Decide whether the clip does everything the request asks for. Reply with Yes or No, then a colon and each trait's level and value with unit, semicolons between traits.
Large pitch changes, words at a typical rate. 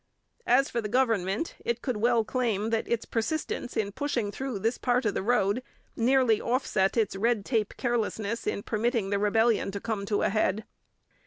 No: average, 2.9 semitones; average, 180 wpm